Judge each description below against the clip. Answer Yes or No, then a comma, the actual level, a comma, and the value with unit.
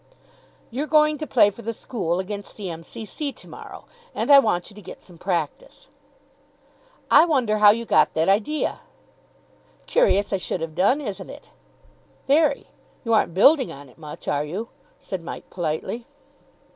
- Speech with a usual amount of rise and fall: No, wide, 7.6 semitones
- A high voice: Yes, high, 210 Hz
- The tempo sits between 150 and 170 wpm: Yes, average, 165 wpm